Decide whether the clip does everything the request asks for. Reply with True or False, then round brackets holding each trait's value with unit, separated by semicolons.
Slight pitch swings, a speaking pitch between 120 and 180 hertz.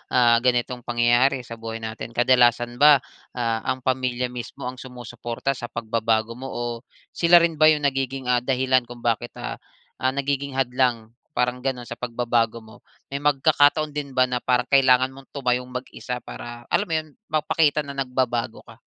True (2.1 semitones; 125 Hz)